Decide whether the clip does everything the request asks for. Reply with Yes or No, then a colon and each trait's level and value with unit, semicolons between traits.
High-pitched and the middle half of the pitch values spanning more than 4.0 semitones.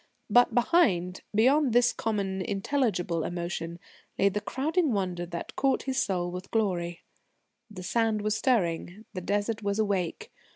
Yes: high, 205 Hz; average, 5.0 semitones